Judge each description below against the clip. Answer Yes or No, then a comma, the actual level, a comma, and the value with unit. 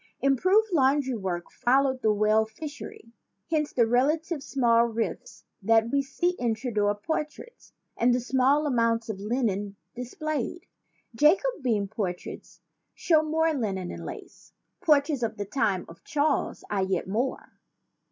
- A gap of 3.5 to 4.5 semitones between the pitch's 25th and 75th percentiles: No, average, 5.2 semitones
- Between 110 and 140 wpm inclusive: Yes, slow, 135 wpm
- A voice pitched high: Yes, high, 245 Hz